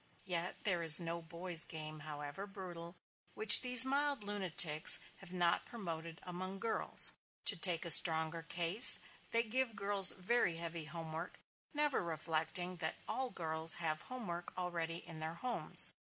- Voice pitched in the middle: Yes, medium, 175 Hz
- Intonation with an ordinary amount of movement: Yes, average, 3.5 semitones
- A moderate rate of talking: Yes, average, 155 wpm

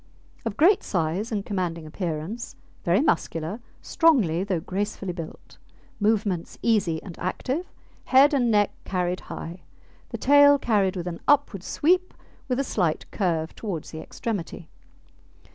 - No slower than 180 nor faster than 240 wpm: No, slow, 135 wpm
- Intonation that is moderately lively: No, wide, 6.0 semitones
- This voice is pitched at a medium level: No, high, 195 Hz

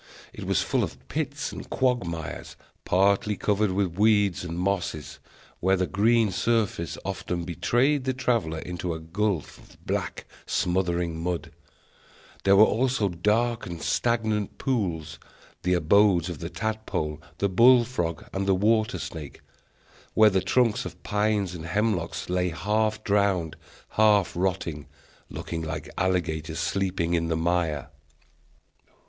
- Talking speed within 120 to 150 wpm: Yes, slow, 135 wpm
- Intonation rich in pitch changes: No, average, 4.2 semitones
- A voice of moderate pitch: No, very low, 95 Hz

